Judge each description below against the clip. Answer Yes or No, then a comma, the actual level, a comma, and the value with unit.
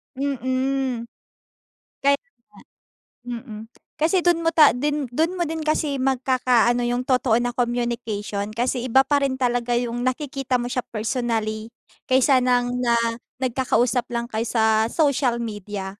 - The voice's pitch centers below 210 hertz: No, high, 245 Hz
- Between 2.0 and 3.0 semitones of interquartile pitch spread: Yes, narrow, 2.5 semitones